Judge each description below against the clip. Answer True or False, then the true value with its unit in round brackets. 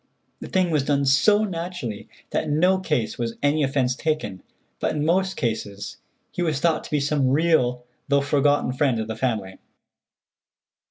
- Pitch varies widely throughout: False (4.5 semitones)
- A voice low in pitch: False (145 Hz)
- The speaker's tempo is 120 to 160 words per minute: False (170 wpm)